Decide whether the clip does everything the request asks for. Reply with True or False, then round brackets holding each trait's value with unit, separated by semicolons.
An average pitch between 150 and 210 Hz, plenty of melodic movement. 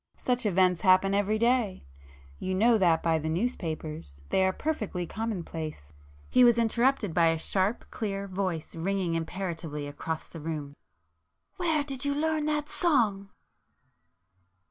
True (190 Hz; 6.3 semitones)